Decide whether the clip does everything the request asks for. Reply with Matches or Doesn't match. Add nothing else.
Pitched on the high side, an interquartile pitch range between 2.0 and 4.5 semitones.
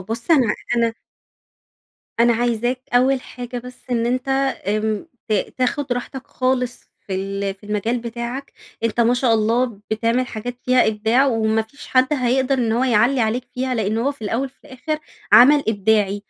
Matches